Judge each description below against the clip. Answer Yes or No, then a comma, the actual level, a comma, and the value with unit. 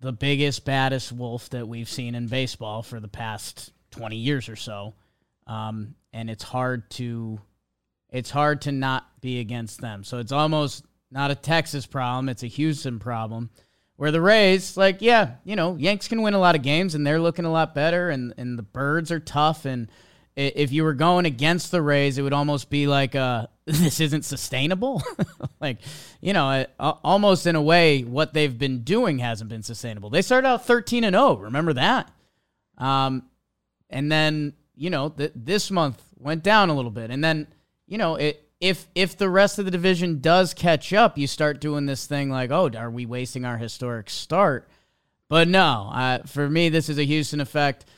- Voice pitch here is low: No, medium, 145 Hz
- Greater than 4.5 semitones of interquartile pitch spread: Yes, average, 5.1 semitones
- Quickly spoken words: No, average, 195 wpm